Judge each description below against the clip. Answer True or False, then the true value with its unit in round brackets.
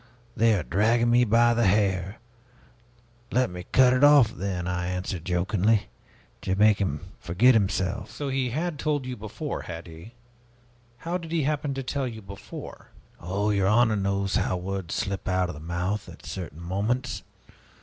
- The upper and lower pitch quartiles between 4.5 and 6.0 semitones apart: True (4.9 semitones)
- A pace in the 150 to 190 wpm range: True (170 wpm)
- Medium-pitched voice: False (100 Hz)